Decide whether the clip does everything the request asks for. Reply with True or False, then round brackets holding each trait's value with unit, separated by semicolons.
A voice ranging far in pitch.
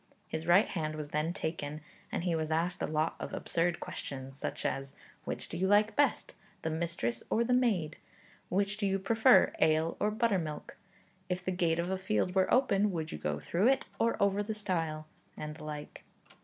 False (4.5 semitones)